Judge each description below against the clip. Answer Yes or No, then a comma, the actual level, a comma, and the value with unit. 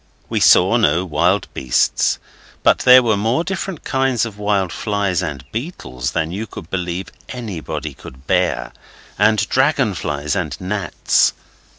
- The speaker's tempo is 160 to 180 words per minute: No, average, 145 wpm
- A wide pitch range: Yes, wide, 5.7 semitones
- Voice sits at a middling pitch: No, low, 100 Hz